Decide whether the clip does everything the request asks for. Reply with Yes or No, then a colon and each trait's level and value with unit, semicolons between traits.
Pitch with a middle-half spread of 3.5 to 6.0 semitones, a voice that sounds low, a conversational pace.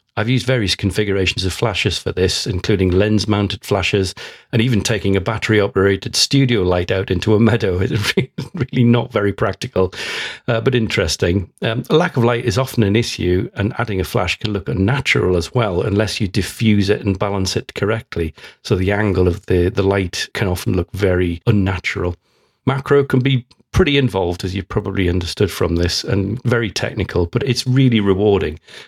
Yes: average, 3.9 semitones; low, 105 Hz; average, 185 wpm